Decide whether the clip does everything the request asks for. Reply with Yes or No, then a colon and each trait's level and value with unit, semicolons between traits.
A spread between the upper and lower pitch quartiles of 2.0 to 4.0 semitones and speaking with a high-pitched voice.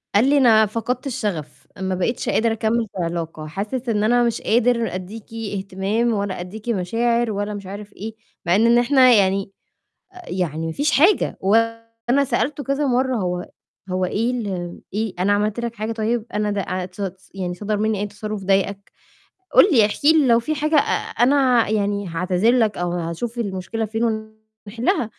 Yes: average, 3.5 semitones; high, 215 Hz